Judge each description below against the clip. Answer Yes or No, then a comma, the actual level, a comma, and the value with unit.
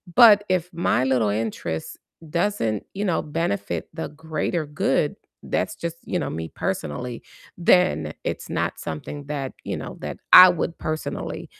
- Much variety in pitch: Yes, wide, 6.6 semitones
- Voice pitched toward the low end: No, medium, 155 Hz